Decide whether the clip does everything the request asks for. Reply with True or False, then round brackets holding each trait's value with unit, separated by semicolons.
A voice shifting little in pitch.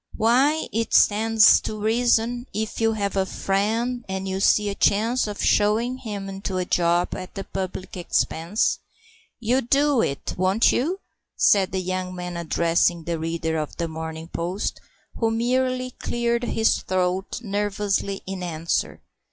False (4.0 semitones)